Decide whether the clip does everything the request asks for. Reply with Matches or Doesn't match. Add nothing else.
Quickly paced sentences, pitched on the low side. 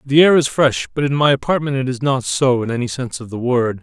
Matches